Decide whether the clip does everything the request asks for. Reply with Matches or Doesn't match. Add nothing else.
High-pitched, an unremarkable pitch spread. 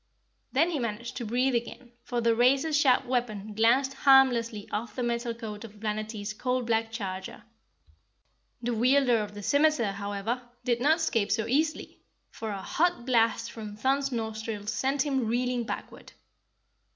Matches